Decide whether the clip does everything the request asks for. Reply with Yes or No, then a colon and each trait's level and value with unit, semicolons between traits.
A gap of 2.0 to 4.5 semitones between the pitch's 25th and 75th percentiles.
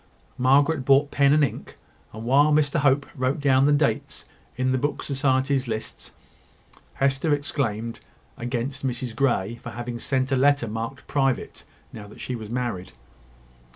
Yes: average, 3.0 semitones